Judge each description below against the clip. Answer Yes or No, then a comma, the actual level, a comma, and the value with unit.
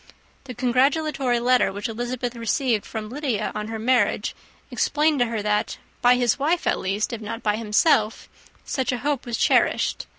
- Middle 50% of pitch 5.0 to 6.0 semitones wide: No, average, 3.0 semitones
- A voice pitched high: Yes, high, 240 Hz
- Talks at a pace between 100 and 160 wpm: No, average, 170 wpm